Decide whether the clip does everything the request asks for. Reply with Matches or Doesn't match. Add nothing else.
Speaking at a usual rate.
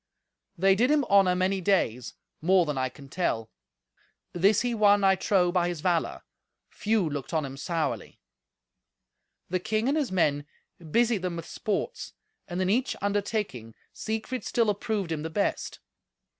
Matches